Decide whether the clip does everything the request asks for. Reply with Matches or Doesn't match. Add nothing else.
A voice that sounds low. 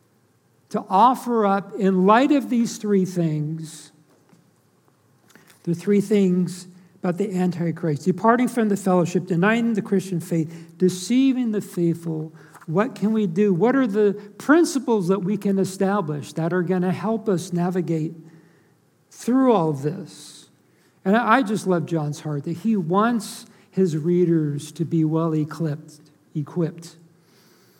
Doesn't match